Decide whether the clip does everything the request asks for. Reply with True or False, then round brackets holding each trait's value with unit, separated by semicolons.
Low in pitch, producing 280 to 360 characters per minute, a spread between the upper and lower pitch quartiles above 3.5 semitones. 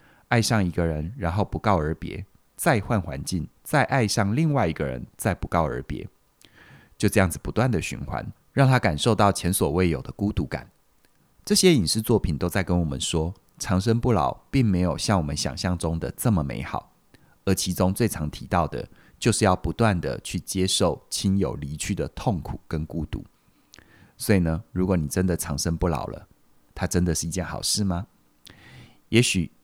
False (90 Hz; 265 characters per minute; 4.4 semitones)